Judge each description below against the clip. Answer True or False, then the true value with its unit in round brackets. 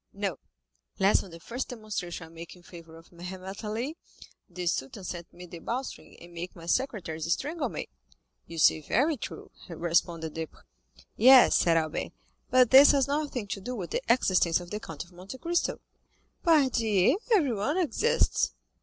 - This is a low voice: False (190 Hz)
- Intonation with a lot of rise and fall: True (7.1 semitones)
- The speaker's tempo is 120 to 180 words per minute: True (165 wpm)